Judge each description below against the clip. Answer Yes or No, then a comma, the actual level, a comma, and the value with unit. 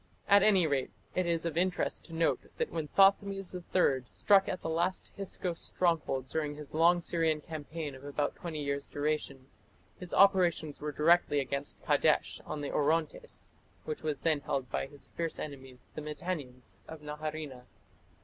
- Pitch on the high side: No, medium, 155 Hz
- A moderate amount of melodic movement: Yes, average, 3.3 semitones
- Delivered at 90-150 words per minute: No, average, 165 wpm